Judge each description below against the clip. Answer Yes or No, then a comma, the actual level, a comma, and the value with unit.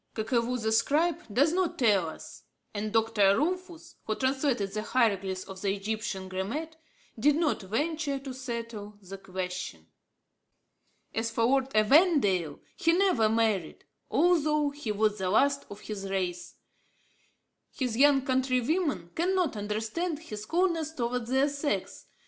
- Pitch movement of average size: No, wide, 6.2 semitones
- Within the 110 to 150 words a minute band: Yes, slow, 135 wpm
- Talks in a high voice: Yes, high, 235 Hz